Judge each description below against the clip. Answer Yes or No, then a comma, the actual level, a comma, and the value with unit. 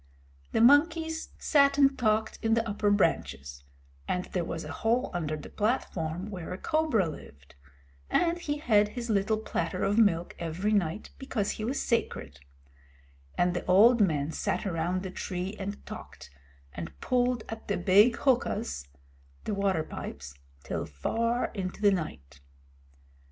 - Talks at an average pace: Yes, average, 150 wpm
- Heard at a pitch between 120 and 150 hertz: No, high, 200 Hz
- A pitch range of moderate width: No, wide, 5.8 semitones